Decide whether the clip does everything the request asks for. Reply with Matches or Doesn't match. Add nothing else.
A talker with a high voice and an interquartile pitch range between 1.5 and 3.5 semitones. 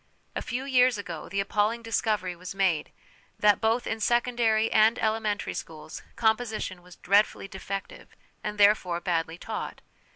Matches